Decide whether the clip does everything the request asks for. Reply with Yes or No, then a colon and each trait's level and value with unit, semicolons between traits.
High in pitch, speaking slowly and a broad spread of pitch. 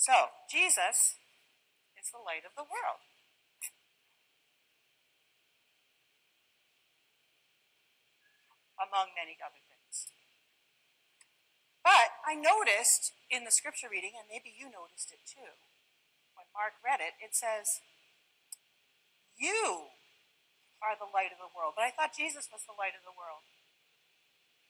Yes: high, 230 Hz; slow, 115 wpm; wide, 8.1 semitones